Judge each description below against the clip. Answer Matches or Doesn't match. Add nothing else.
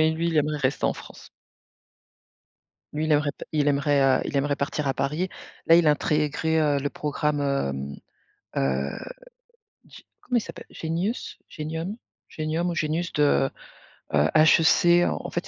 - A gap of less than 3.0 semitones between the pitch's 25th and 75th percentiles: Matches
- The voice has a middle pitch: Matches